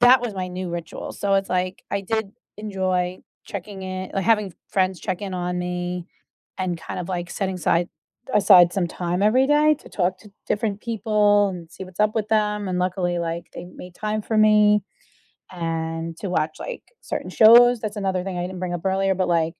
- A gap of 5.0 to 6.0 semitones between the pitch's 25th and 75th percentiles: No, average, 2.8 semitones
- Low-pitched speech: No, high, 190 Hz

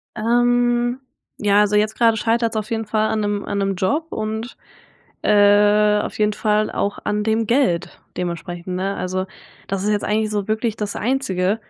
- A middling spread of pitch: No, narrow, 1.8 semitones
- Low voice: No, high, 210 Hz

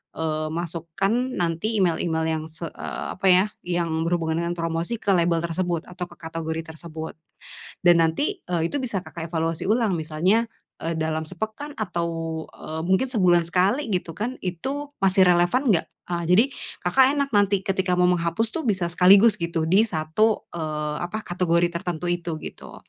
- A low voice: No, medium, 175 Hz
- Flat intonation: No, average, 3.5 semitones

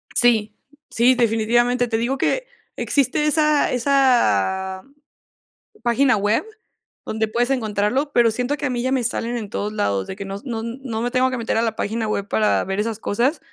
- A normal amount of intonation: Yes, average, 3.2 semitones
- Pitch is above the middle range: Yes, high, 235 Hz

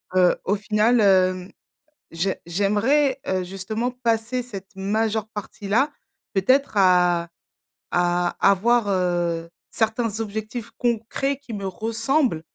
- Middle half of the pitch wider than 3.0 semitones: Yes, average, 4.0 semitones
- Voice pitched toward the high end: Yes, high, 210 Hz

